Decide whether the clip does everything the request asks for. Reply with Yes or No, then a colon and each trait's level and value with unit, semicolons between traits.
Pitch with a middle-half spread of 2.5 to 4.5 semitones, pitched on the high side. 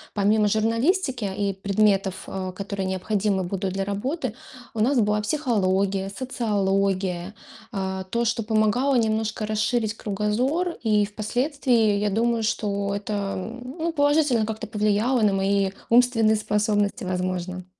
Yes: average, 3.0 semitones; high, 210 Hz